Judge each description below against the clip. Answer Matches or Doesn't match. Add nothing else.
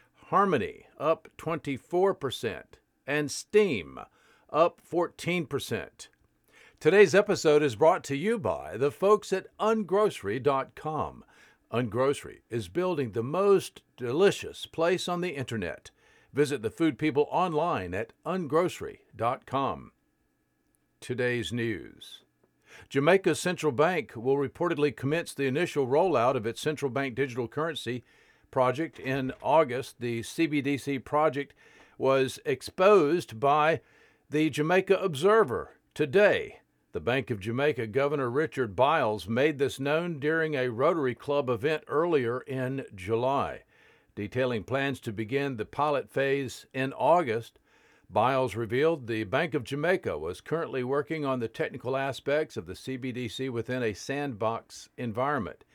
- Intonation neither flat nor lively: Matches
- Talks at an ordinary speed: Doesn't match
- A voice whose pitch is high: Doesn't match